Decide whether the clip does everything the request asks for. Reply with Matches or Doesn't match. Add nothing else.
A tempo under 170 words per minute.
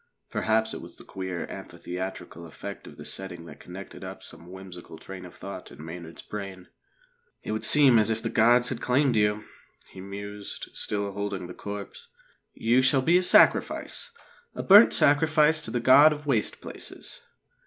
Doesn't match